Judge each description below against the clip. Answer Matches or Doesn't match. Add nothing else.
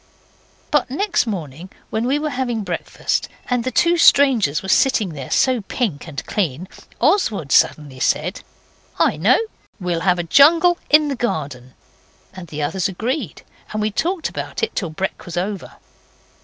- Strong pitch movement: Matches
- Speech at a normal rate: Matches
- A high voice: Matches